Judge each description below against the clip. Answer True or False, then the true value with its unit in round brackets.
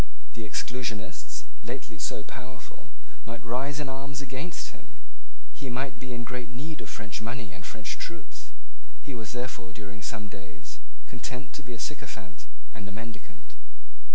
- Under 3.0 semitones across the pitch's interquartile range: False (3.9 semitones)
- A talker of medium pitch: False (120 Hz)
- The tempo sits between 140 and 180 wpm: True (155 wpm)